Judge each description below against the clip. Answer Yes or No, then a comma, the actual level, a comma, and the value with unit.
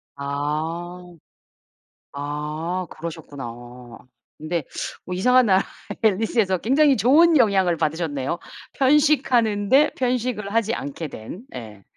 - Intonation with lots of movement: Yes, wide, 7.7 semitones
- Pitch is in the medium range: Yes, medium, 180 Hz